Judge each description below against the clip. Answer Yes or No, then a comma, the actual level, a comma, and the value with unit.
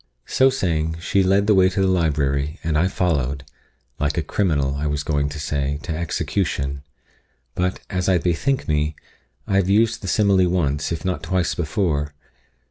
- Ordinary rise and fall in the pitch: Yes, average, 4.3 semitones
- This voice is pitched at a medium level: No, very low, 85 Hz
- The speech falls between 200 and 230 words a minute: No, average, 175 wpm